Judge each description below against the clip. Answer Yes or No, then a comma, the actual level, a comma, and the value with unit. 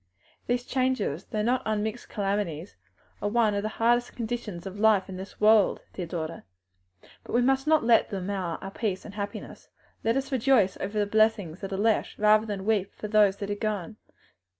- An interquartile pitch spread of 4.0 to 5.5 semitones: No, narrow, 2.6 semitones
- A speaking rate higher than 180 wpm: Yes, average, 195 wpm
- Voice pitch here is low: No, high, 210 Hz